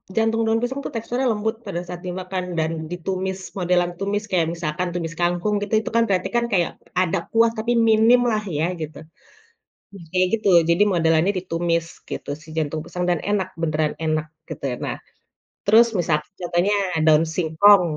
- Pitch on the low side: No, medium, 180 Hz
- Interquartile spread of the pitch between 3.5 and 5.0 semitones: Yes, average, 4.1 semitones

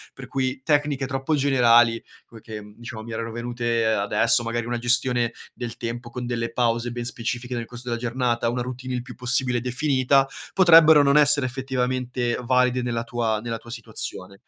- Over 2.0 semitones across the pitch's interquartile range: No, narrow, 1.7 semitones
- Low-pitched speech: Yes, low, 120 Hz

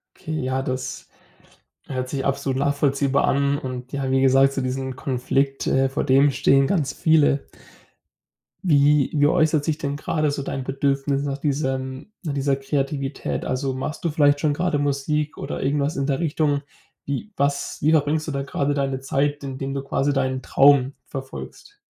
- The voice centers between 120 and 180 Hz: Yes, medium, 140 Hz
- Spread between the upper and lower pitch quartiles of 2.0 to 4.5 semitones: No, narrow, 1.4 semitones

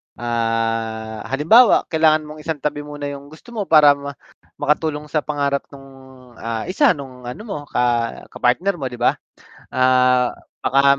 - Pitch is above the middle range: No, medium, 140 Hz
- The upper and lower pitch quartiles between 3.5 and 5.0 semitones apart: Yes, average, 3.8 semitones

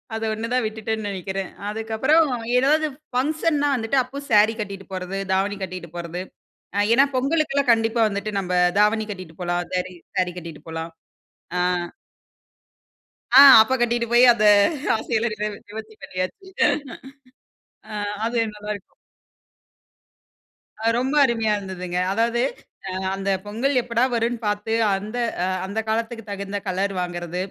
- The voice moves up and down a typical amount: Yes, average, 3.6 semitones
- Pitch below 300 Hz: Yes, high, 215 Hz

